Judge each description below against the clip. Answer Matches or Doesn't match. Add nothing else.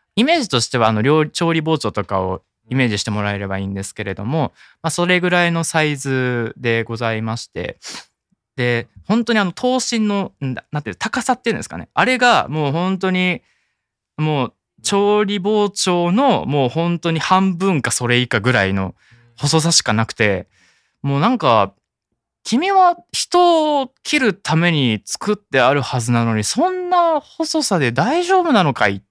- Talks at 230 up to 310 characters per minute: Doesn't match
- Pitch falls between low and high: Matches